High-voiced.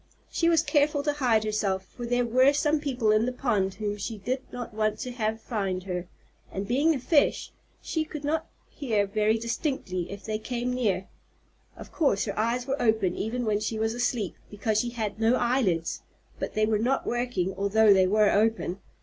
Yes: high, 225 Hz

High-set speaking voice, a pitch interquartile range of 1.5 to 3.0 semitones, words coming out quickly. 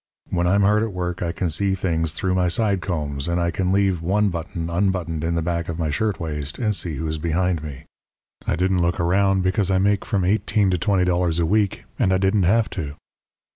No: very low, 90 Hz; narrow, 2.6 semitones; fast, 220 wpm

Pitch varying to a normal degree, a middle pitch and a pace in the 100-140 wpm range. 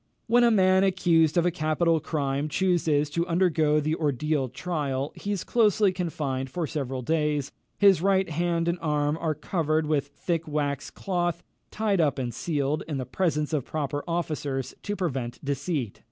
No: average, 3.5 semitones; medium, 155 Hz; average, 170 wpm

